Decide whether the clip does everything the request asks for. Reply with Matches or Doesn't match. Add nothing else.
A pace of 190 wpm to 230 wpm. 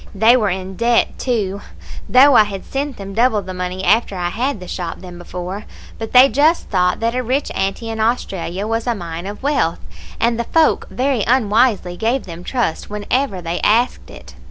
Matches